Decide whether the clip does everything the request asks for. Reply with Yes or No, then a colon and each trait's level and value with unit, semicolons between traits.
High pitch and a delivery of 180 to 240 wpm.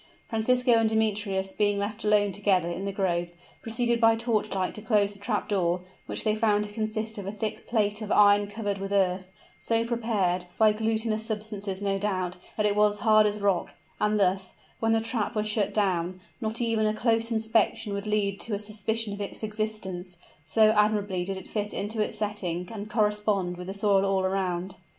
Yes: high, 210 Hz; average, 195 wpm